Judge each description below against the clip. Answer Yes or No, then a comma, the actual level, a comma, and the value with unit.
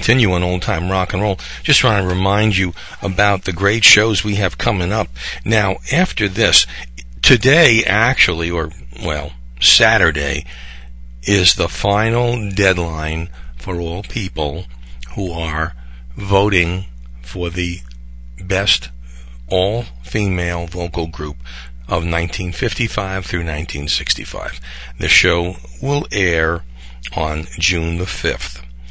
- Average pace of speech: No, slow, 120 wpm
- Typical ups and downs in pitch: No, wide, 8.1 semitones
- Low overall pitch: Yes, very low, 85 Hz